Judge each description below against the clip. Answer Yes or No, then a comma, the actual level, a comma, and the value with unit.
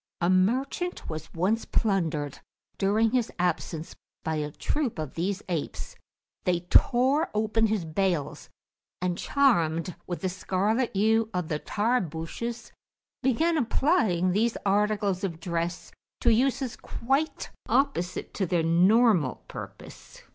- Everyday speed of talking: No, slow, 125 wpm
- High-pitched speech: Yes, high, 195 Hz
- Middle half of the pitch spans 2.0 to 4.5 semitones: No, wide, 5.4 semitones